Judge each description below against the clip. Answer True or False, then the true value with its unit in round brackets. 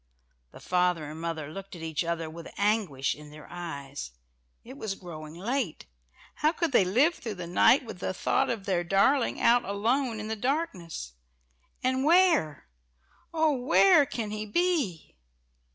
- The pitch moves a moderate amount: False (7.6 semitones)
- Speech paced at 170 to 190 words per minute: False (160 wpm)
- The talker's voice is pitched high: True (200 Hz)